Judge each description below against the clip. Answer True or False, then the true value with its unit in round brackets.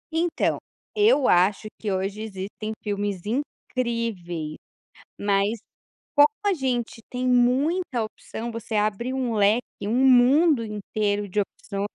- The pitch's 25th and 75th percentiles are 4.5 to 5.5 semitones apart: False (3.9 semitones)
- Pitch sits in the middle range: False (225 Hz)